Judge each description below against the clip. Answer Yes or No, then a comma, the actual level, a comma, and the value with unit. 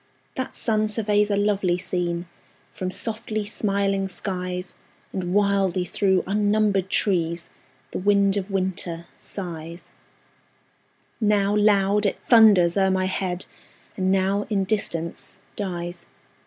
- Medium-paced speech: No, slow, 115 wpm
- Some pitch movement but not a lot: No, narrow, 2.3 semitones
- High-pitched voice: Yes, high, 195 Hz